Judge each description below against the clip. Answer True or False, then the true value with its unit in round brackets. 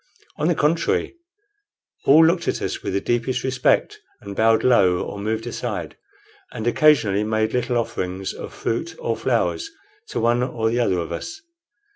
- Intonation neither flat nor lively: True (4.1 semitones)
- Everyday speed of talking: True (165 wpm)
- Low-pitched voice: True (120 Hz)